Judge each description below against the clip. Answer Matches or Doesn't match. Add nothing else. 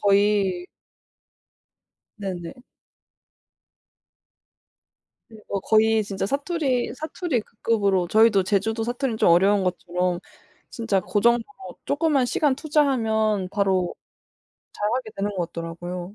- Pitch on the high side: Matches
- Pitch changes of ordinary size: Matches